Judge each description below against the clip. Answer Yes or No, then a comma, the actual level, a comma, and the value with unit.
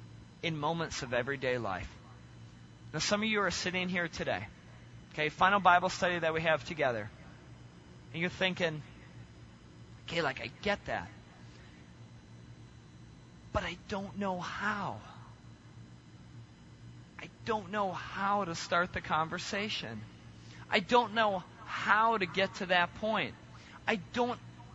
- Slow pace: Yes, slow, 130 wpm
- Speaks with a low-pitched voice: No, medium, 160 Hz